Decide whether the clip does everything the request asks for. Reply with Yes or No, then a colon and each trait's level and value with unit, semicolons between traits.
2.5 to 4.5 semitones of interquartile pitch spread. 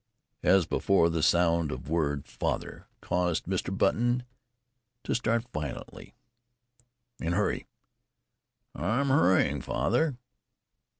No: wide, 5.5 semitones